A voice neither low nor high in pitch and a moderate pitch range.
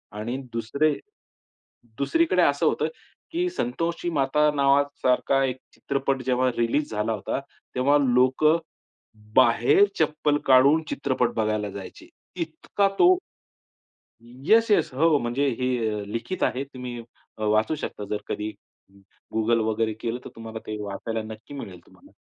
No: low, 130 Hz; average, 4.8 semitones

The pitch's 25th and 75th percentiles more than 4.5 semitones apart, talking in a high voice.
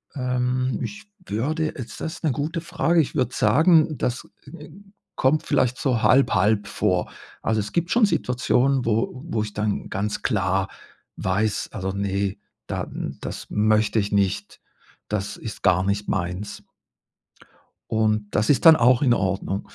No: average, 5.2 semitones; low, 110 Hz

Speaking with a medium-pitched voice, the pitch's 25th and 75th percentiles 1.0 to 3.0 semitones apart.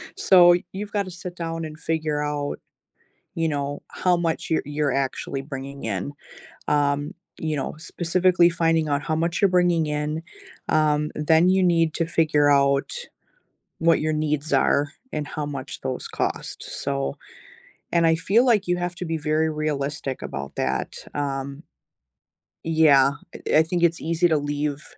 Yes: medium, 155 Hz; narrow, 2.6 semitones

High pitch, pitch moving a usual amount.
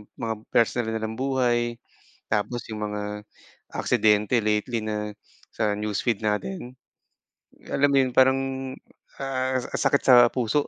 No: low, 115 Hz; average, 3.4 semitones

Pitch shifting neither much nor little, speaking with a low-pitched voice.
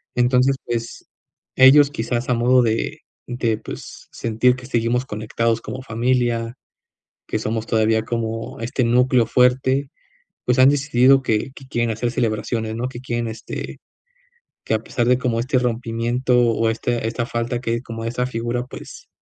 No: narrow, 1.8 semitones; low, 120 Hz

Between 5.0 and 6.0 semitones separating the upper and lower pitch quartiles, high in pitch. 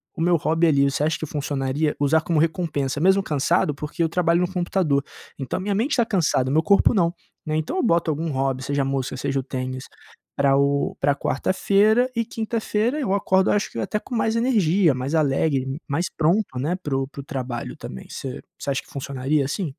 No: average, 5.3 semitones; medium, 155 Hz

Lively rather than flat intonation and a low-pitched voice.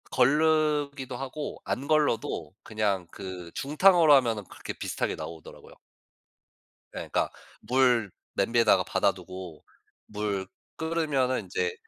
Yes: wide, 6.5 semitones; low, 130 Hz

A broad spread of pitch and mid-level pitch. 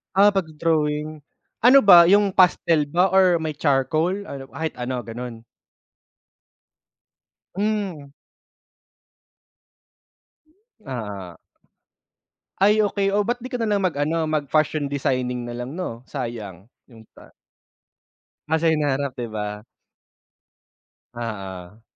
Yes: wide, 7.1 semitones; medium, 150 Hz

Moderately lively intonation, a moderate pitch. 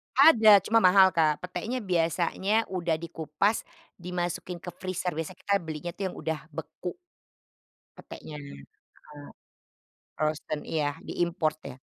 Yes: average, 3.2 semitones; medium, 175 Hz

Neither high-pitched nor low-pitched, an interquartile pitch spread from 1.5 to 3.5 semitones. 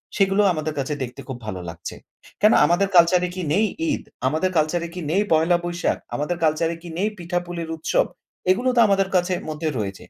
Yes: medium, 175 Hz; average, 3.1 semitones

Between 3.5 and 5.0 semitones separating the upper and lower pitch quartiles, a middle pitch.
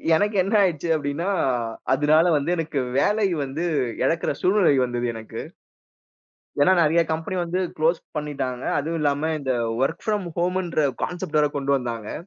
Yes: average, 4.0 semitones; medium, 160 Hz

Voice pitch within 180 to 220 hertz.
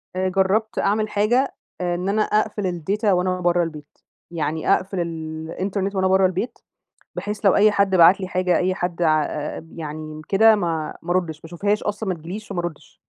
Yes: medium, 185 Hz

